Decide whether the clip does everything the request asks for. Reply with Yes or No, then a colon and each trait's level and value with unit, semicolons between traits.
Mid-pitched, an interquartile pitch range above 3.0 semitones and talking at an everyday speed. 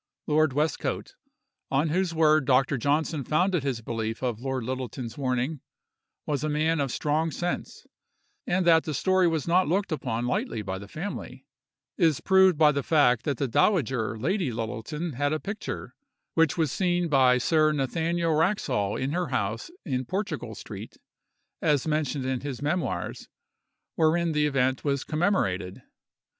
Yes: medium, 150 Hz; average, 4.3 semitones; average, 150 wpm